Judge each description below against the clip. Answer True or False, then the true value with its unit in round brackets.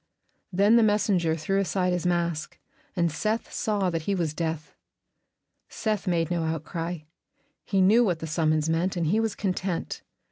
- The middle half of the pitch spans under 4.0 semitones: True (3.4 semitones)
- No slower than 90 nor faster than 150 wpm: False (165 wpm)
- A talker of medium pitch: True (175 Hz)